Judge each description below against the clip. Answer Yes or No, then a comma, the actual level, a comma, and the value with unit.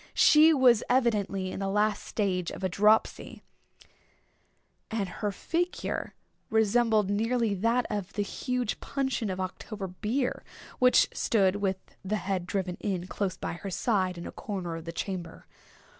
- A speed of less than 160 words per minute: Yes, average, 150 wpm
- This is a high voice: Yes, high, 205 Hz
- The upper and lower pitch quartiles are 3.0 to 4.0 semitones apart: Yes, average, 3.5 semitones